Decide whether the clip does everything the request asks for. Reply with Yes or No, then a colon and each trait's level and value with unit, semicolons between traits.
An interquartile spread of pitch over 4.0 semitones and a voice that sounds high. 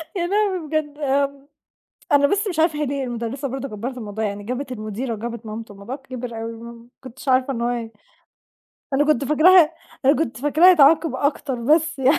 Yes: average, 4.4 semitones; very high, 270 Hz